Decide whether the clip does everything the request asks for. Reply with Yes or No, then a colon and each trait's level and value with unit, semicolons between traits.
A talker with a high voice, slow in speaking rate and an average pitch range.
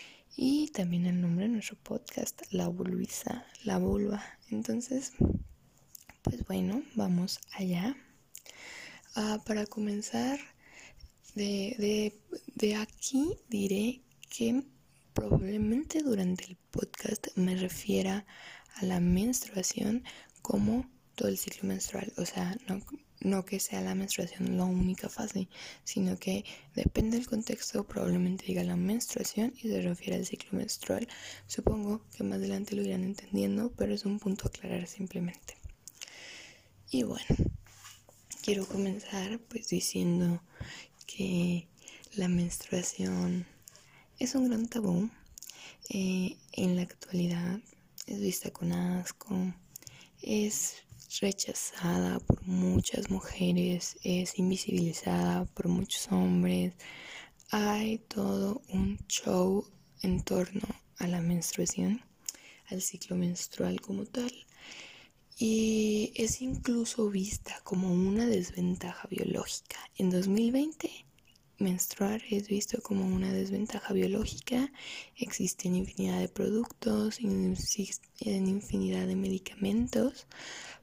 Yes: high, 195 Hz; slow, 110 wpm; average, 3.4 semitones